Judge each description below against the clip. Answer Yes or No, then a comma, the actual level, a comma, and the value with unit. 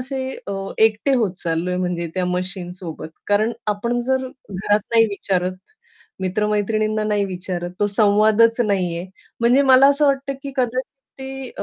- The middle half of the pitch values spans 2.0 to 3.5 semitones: No, average, 5.2 semitones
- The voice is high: Yes, high, 210 Hz